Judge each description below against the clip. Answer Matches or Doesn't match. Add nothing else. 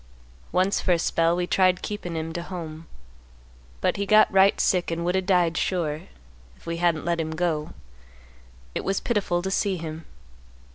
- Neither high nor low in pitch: Matches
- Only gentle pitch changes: Matches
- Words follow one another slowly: Doesn't match